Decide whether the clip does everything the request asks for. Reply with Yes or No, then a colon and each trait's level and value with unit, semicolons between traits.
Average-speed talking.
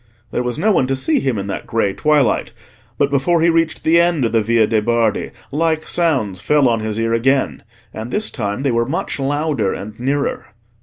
No: fast, 210 wpm